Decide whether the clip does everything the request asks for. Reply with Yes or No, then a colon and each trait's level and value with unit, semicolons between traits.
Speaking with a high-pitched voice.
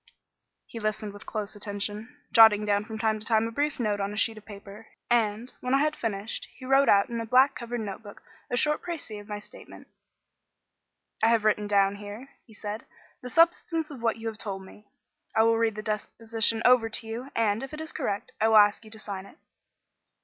Yes: high, 220 Hz